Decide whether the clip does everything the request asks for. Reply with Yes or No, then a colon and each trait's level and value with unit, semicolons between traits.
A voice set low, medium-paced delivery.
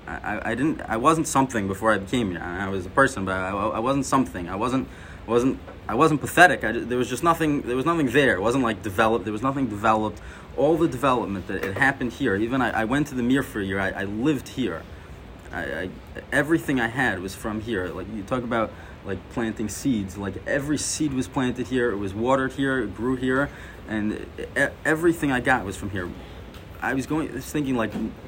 No: low, 115 Hz; fast, 240 wpm